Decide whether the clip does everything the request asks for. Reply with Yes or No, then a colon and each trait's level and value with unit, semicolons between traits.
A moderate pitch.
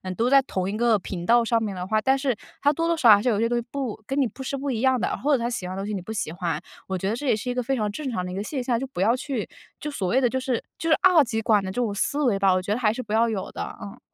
No: high, 230 Hz